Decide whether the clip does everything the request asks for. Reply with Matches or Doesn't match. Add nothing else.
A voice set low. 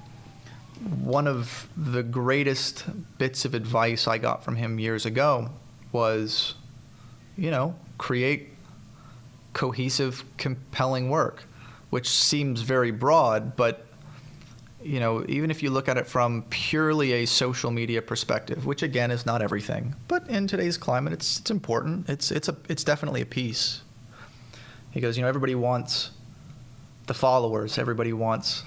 Matches